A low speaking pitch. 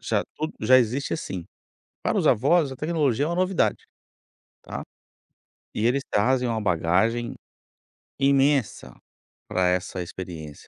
Yes: low, 125 Hz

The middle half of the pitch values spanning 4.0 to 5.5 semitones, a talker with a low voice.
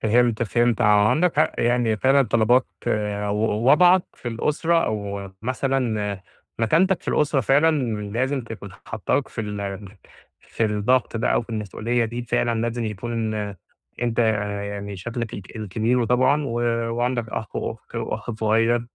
No: average, 2.8 semitones; low, 115 Hz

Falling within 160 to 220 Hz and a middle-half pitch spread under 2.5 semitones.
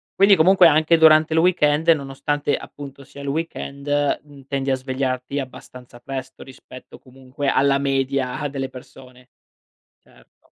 No: medium, 140 Hz; narrow, 2.1 semitones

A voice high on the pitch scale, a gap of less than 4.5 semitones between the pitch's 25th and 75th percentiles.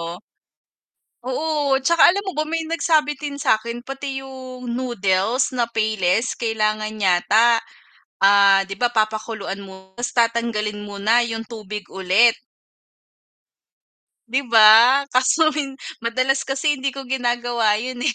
Yes: high, 235 Hz; average, 3.9 semitones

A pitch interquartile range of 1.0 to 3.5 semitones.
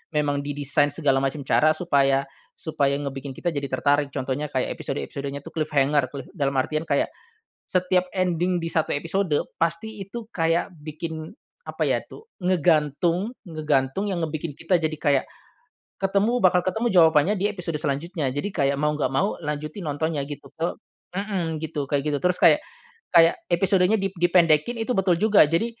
No: average, 3.9 semitones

